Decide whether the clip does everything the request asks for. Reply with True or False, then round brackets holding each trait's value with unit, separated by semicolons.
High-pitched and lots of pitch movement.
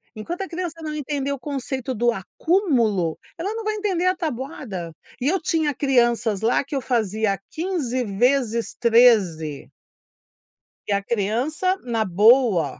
True (250 Hz; 6.2 semitones)